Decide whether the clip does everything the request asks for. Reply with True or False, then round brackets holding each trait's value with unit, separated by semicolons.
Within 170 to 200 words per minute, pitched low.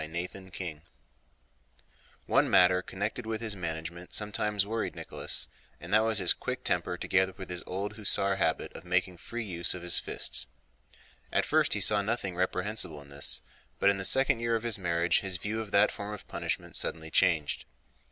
True (180 wpm; 95 Hz)